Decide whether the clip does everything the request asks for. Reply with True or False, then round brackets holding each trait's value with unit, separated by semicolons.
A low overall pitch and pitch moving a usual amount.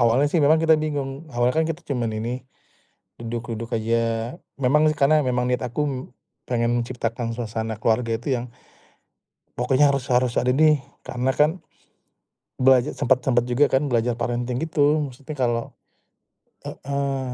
True (125 Hz; 3.0 semitones)